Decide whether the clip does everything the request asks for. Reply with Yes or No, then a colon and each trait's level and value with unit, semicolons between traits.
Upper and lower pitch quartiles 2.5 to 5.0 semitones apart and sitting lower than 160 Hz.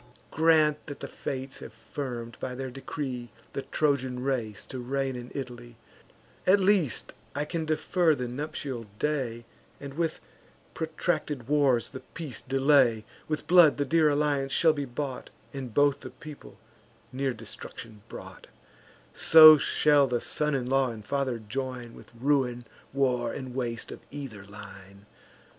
Yes: average, 3.5 semitones; low, 135 Hz